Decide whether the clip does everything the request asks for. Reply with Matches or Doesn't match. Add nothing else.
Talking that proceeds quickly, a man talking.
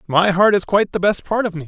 Matches